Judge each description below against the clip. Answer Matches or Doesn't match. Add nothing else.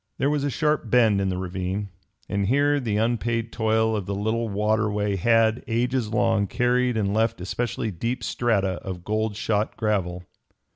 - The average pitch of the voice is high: Doesn't match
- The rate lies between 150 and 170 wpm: Matches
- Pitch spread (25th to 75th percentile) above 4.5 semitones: Doesn't match